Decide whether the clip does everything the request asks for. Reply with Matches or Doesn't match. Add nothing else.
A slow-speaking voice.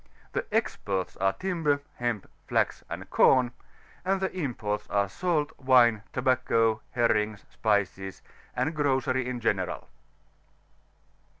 Matches